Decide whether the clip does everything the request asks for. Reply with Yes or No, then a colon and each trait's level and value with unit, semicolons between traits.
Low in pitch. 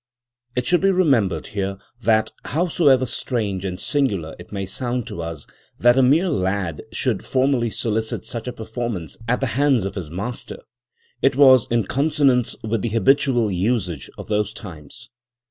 Yes: low, 115 Hz